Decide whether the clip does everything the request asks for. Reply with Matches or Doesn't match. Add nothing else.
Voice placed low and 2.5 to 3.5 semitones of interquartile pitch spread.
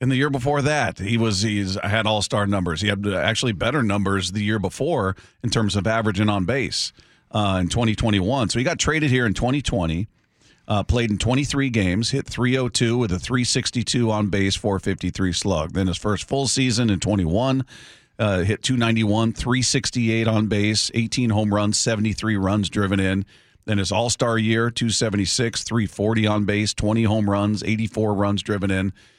Matches